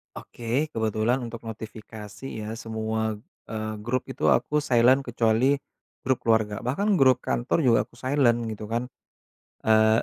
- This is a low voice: Yes, low, 115 Hz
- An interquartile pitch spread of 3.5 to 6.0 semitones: No, average, 2.7 semitones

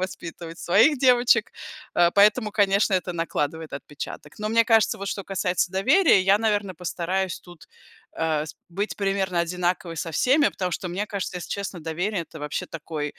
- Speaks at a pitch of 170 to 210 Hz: Yes, medium, 185 Hz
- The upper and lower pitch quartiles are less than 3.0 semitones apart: No, average, 3.5 semitones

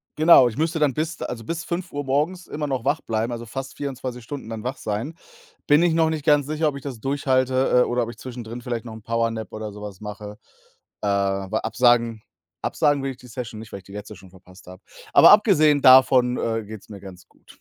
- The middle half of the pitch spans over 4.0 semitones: Yes, average, 4.8 semitones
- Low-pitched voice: Yes, low, 125 Hz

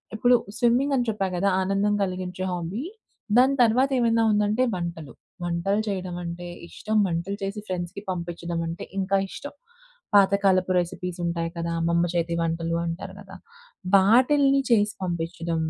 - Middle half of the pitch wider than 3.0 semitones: Yes, average, 3.7 semitones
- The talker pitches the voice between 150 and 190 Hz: Yes, medium, 185 Hz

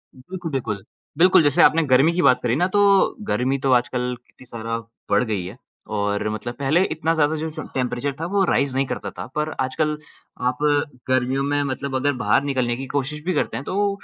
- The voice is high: No, low, 135 Hz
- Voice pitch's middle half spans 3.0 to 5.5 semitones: Yes, average, 3.6 semitones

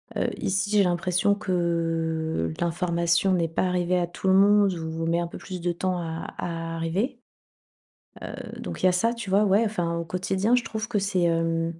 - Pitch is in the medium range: Yes, medium, 175 Hz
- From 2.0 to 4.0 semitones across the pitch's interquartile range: Yes, average, 2.7 semitones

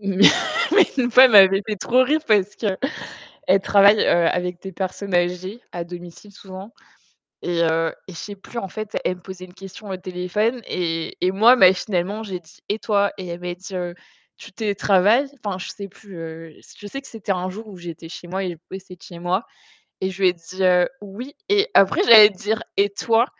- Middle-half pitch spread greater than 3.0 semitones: No, average, 2.7 semitones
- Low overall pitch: No, high, 190 Hz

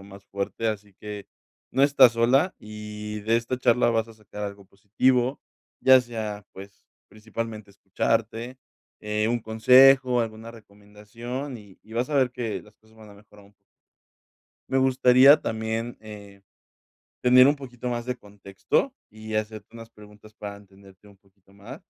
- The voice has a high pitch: No, low, 110 Hz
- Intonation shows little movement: No, average, 3.0 semitones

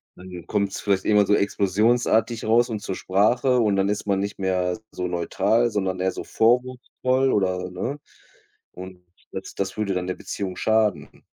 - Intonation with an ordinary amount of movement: Yes, average, 3.2 semitones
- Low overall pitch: Yes, low, 100 Hz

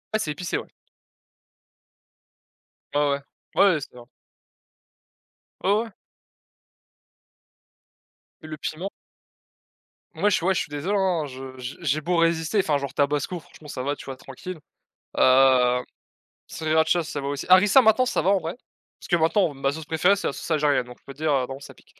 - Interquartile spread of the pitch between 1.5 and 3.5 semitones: No, average, 4.3 semitones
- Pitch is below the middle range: No, medium, 155 Hz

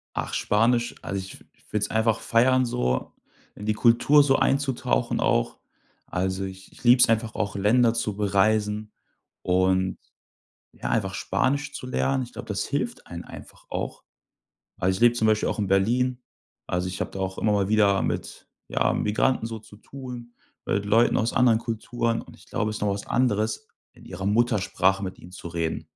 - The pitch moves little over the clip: No, average, 3.7 semitones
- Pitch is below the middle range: Yes, low, 110 Hz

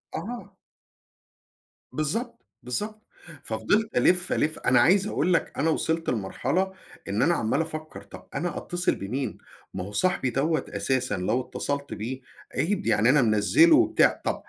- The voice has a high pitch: No, medium, 155 Hz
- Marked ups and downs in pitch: Yes, wide, 7.1 semitones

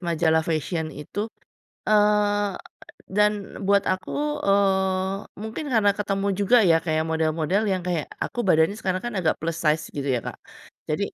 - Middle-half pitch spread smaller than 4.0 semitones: No, average, 4.3 semitones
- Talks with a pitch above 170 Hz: Yes, high, 190 Hz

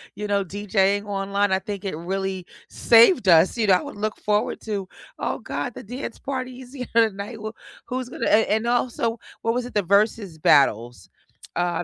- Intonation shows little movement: No, average, 3.2 semitones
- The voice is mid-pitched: No, high, 205 Hz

